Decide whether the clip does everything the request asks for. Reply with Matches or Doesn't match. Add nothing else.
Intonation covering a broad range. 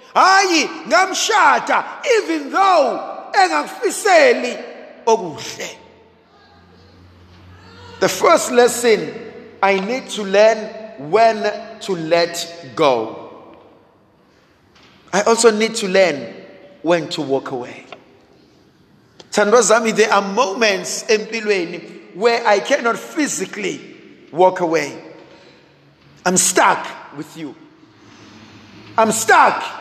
Matches